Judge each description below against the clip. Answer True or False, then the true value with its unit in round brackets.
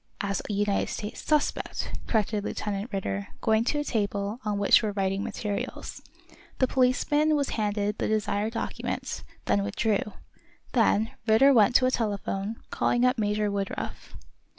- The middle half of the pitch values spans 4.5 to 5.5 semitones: False (2.7 semitones)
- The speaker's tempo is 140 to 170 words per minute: True (150 wpm)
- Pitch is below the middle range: False (210 Hz)